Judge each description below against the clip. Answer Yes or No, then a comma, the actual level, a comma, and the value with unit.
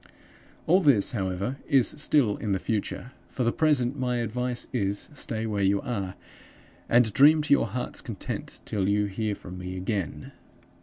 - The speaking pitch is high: No, low, 115 Hz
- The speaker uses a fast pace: No, average, 165 wpm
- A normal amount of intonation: Yes, average, 4.2 semitones